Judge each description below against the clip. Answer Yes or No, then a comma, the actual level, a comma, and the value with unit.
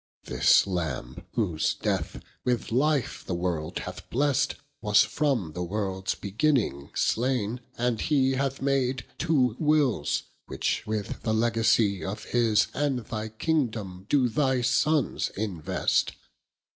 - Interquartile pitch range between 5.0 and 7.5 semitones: Yes, wide, 5.5 semitones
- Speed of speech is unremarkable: No, slow, 125 wpm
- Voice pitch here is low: Yes, low, 115 Hz